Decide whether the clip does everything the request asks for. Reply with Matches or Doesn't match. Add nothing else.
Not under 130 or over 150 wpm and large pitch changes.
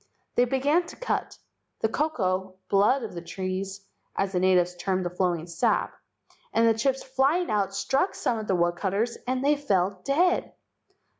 Doesn't match